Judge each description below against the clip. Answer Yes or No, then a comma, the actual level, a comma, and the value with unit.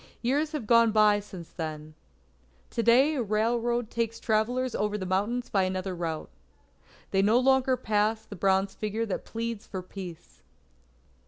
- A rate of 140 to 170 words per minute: Yes, average, 155 wpm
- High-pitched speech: Yes, high, 215 Hz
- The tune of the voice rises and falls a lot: No, average, 3.5 semitones